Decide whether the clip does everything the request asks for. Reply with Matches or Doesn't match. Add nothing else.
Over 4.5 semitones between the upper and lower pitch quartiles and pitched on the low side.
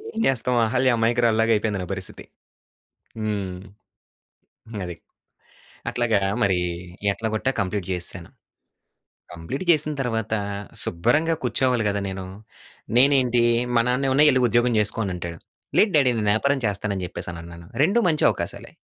Matches